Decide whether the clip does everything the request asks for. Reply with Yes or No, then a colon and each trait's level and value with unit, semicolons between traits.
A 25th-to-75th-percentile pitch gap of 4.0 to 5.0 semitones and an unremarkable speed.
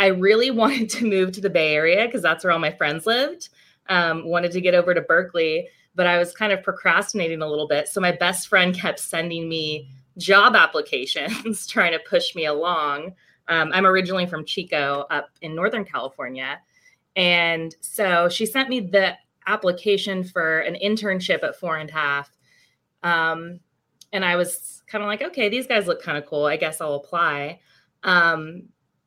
Yes: average, 4.3 semitones; average, 185 wpm